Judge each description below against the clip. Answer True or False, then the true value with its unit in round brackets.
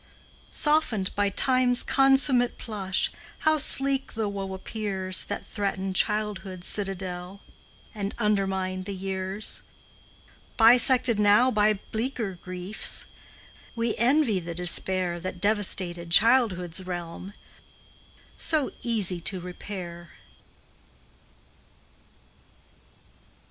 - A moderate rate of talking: False (90 wpm)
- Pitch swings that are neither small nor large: True (3.8 semitones)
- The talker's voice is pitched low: False (200 Hz)